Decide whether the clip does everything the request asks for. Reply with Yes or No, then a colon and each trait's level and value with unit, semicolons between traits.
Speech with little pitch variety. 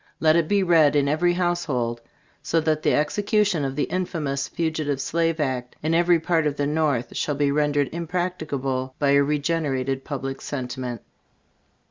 No: average, 3.3 semitones